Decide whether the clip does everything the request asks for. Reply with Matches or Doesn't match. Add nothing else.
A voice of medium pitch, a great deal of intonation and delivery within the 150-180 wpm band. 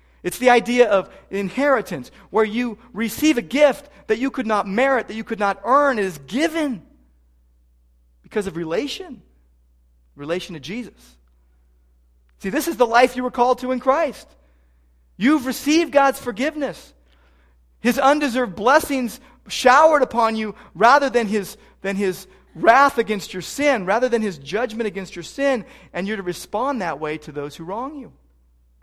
Doesn't match